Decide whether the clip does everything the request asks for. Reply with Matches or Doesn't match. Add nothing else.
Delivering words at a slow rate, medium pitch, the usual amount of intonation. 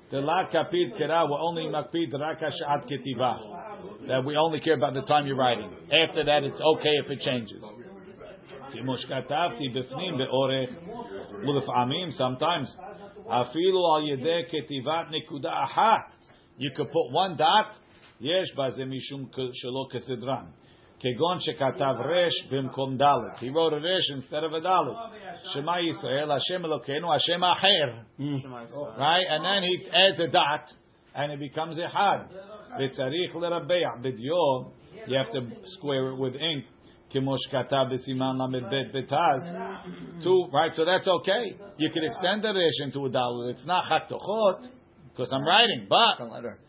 Matches